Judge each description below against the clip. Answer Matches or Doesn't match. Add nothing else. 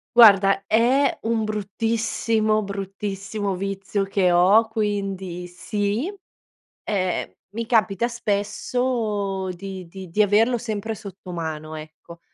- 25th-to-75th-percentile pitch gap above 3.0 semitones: Doesn't match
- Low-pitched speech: Doesn't match